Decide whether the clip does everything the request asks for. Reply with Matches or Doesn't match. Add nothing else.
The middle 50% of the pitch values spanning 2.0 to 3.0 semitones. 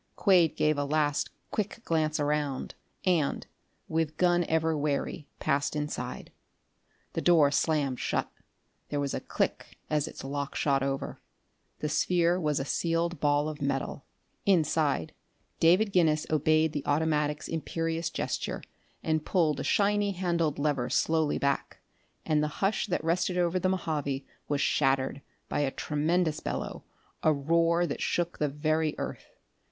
Matches